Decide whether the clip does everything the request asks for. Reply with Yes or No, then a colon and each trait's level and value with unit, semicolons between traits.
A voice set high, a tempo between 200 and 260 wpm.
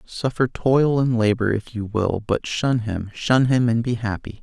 No: low, 115 Hz; fast, 205 wpm